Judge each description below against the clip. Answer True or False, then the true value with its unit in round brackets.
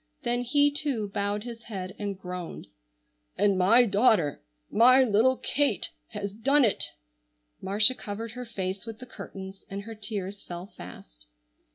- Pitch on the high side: True (210 Hz)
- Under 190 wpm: True (150 wpm)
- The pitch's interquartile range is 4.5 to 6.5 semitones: False (3.8 semitones)